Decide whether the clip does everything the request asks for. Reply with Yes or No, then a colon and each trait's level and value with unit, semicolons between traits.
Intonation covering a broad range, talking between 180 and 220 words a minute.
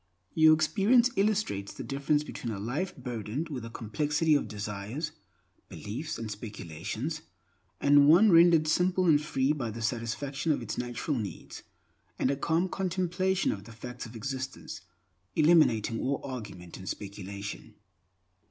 No: wide, 6.4 semitones; average, 145 wpm